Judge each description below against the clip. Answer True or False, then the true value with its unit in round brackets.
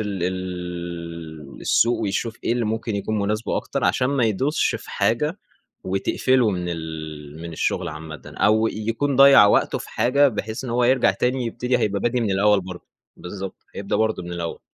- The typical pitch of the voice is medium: False (105 Hz)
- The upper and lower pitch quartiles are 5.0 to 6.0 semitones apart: True (5.4 semitones)